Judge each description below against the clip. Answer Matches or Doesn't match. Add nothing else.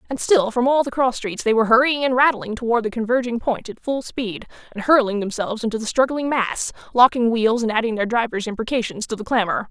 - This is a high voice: Matches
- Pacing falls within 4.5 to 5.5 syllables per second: Doesn't match